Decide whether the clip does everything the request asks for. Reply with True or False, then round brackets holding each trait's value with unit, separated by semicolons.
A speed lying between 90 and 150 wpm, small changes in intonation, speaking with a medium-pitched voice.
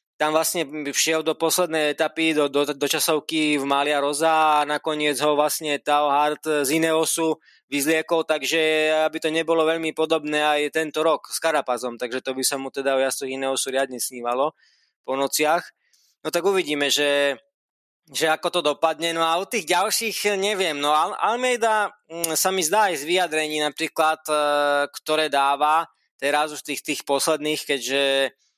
False (160 wpm; 2.1 semitones; 155 Hz)